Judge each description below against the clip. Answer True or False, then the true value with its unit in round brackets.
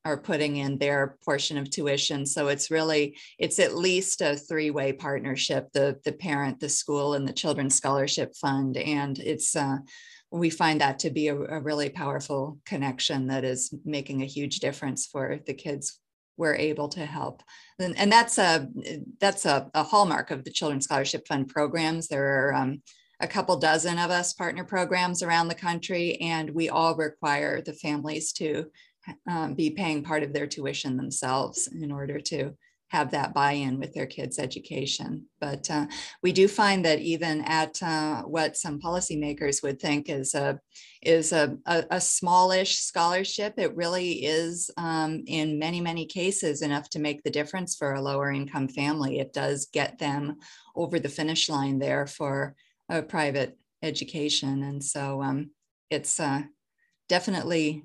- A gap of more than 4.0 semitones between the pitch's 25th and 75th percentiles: False (3.0 semitones)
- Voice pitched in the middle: True (150 Hz)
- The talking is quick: False (170 wpm)